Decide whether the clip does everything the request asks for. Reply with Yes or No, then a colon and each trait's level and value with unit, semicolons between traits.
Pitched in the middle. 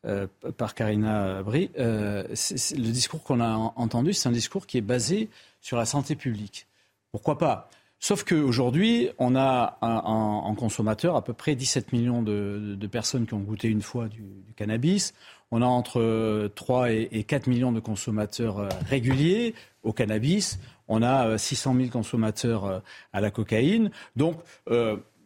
No: low, 115 Hz